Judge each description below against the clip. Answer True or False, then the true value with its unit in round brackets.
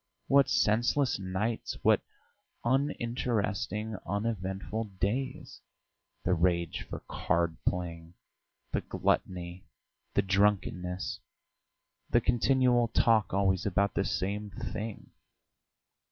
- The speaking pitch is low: True (100 Hz)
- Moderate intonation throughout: True (3.9 semitones)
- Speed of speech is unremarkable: False (90 wpm)